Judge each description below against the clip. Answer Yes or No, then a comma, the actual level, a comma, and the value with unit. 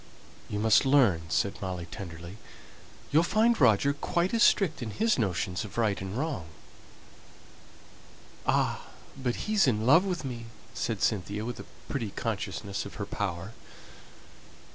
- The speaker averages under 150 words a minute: Yes, average, 140 wpm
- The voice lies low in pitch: Yes, low, 110 Hz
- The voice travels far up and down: Yes, wide, 6.6 semitones